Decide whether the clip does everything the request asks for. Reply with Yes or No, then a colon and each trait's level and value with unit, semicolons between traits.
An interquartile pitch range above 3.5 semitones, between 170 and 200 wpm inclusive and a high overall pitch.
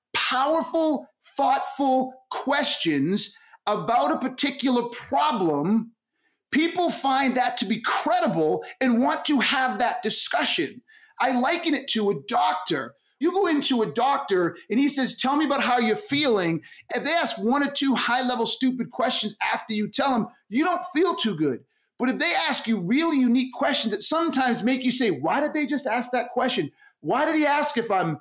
Yes: average, 4.6 semitones; average, 180 wpm; very high, 260 Hz